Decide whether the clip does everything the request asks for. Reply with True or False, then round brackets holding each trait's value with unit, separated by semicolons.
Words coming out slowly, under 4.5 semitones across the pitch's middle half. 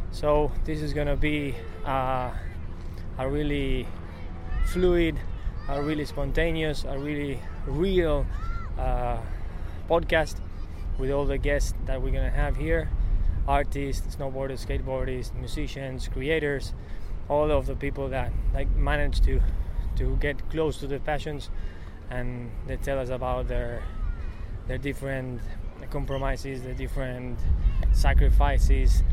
False (115 wpm; 8.5 semitones)